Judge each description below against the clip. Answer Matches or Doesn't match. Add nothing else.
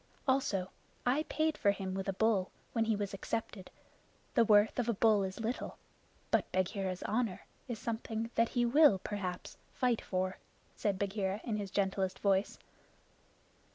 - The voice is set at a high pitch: Matches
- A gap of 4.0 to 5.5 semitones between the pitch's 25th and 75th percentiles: Doesn't match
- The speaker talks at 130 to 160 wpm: Matches